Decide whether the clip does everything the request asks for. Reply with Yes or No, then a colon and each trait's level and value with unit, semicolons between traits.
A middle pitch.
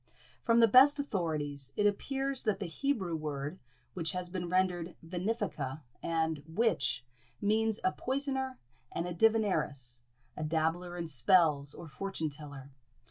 Yes: medium, 175 Hz